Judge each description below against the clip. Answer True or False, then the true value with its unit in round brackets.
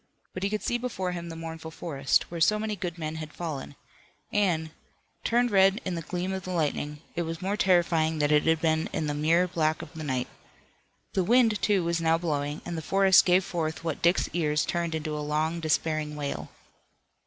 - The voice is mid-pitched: True (165 Hz)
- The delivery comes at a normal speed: False (210 wpm)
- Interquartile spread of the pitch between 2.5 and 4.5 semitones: True (2.9 semitones)